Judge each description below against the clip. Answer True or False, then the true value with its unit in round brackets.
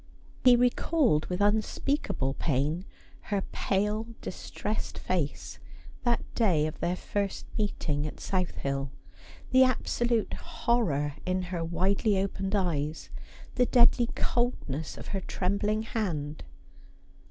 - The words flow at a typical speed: False (115 wpm)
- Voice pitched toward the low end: False (195 Hz)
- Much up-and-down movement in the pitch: True (6.1 semitones)